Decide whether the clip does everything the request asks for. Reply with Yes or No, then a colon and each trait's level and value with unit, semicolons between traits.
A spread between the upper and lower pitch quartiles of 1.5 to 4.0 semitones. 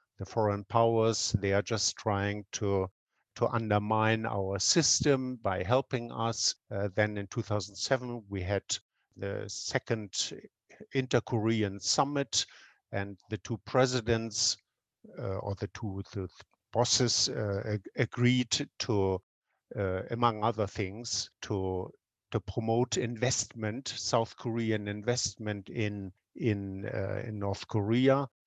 Yes: average, 2.8 semitones